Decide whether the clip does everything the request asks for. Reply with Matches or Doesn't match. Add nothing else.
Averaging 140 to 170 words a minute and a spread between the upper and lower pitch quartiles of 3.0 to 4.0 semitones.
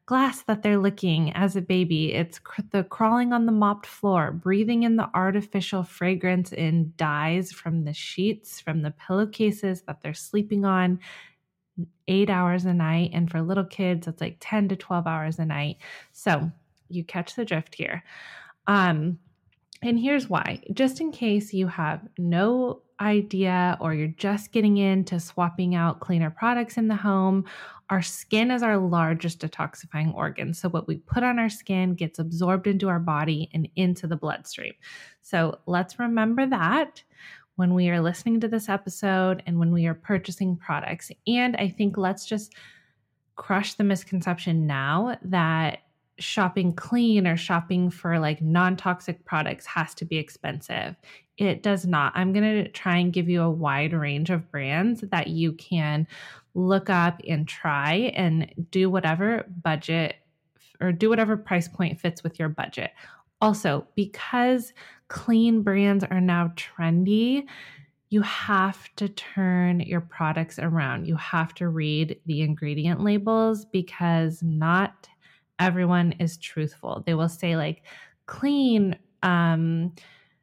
Matches